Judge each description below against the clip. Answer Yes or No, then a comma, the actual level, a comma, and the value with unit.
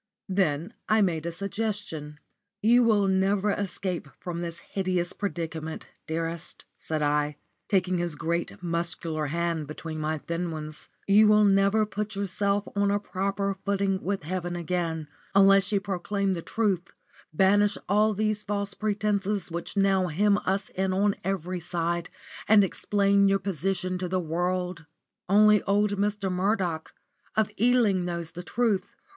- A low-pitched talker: No, high, 190 Hz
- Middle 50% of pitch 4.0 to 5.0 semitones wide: No, average, 3.0 semitones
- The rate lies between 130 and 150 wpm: Yes, average, 145 wpm